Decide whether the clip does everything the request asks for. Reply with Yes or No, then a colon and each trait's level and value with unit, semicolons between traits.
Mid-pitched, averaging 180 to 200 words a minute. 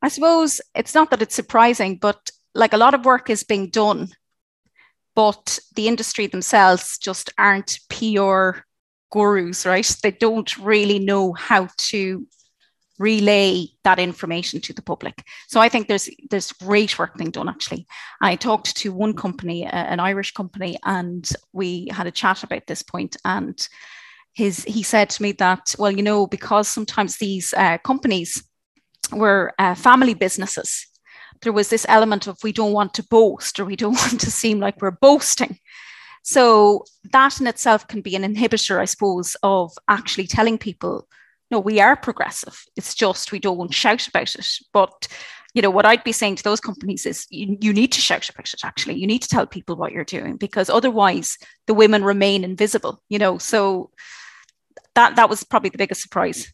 No: high, 205 Hz; average, 185 wpm